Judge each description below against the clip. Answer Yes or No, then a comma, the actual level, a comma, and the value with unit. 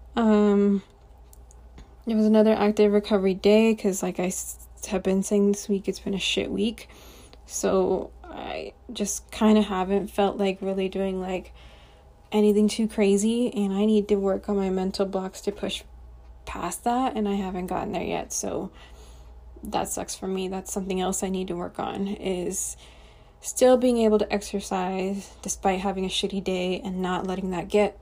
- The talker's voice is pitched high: Yes, high, 195 Hz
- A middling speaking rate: Yes, average, 175 wpm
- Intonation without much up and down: Yes, narrow, 1.8 semitones